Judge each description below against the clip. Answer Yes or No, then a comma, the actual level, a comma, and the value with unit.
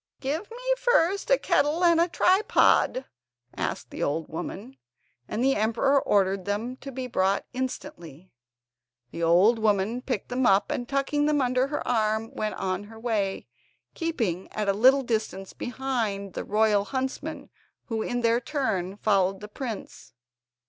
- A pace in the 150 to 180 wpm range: Yes, average, 155 wpm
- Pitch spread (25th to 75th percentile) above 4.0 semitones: Yes, average, 5.3 semitones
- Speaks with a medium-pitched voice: No, high, 230 Hz